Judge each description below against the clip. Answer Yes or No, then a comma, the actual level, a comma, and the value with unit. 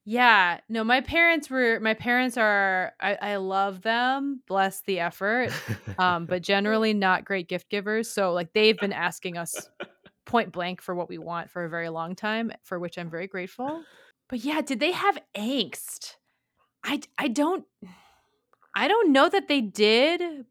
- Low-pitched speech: No, high, 215 Hz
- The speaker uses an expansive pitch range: Yes, wide, 6.1 semitones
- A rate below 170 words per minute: No, average, 175 wpm